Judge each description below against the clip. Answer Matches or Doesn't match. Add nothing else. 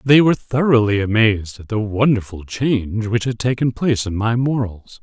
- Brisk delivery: Doesn't match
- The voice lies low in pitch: Matches